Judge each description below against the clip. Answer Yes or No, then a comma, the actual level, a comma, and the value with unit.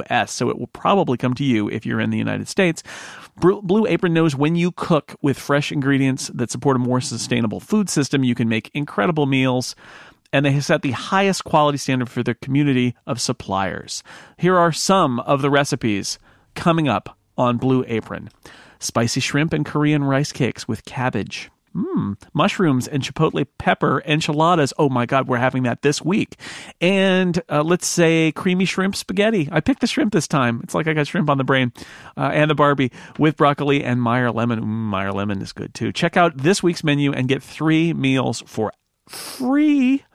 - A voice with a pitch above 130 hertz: Yes, medium, 140 Hz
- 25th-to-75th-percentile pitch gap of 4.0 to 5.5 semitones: Yes, average, 5.0 semitones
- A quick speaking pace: No, average, 190 wpm